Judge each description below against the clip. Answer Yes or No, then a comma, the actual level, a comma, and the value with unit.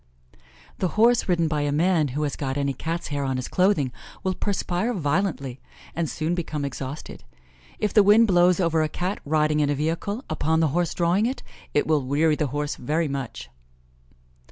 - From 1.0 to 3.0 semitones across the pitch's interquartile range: No, average, 3.9 semitones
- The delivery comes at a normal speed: Yes, average, 185 wpm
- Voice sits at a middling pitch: Yes, medium, 160 Hz